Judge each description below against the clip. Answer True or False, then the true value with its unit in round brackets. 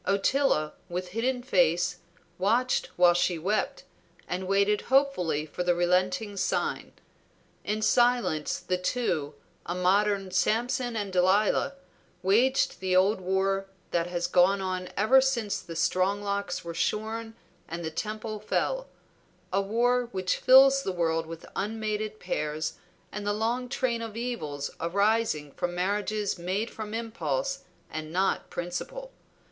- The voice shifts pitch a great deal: False (4.2 semitones)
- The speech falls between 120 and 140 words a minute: True (135 wpm)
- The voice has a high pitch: True (200 Hz)